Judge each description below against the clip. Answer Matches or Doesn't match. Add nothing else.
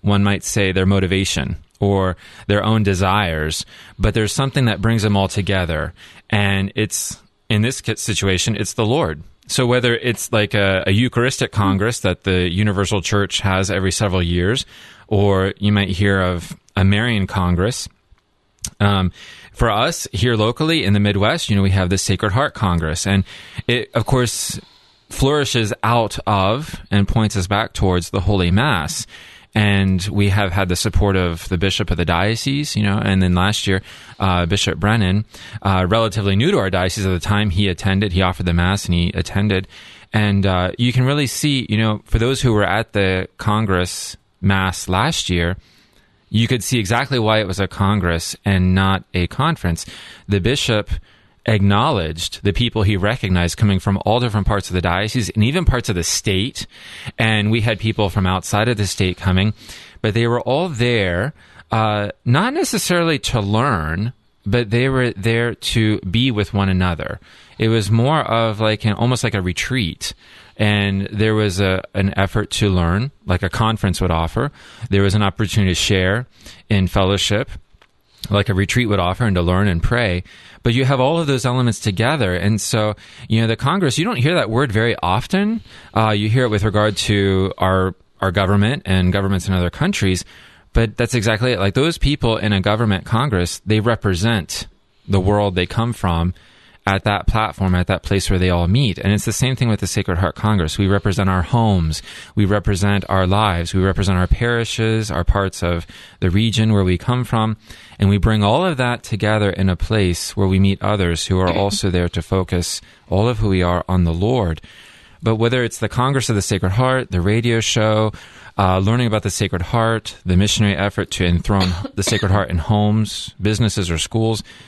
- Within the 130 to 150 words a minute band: Doesn't match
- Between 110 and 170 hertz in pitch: Doesn't match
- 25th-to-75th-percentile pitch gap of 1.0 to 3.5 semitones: Matches